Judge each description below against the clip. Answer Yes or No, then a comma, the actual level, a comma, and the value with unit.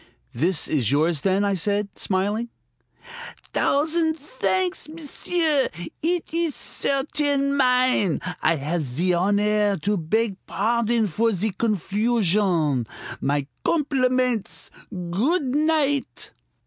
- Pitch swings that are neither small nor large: No, wide, 7.1 semitones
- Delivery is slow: Yes, slow, 100 wpm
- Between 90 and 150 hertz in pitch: No, high, 215 Hz